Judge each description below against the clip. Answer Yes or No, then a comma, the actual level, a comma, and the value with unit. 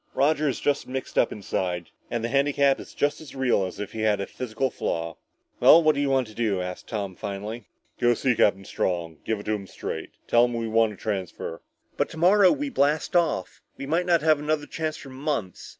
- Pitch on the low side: Yes, low, 120 Hz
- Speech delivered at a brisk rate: Yes, fast, 220 wpm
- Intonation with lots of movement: Yes, wide, 6.3 semitones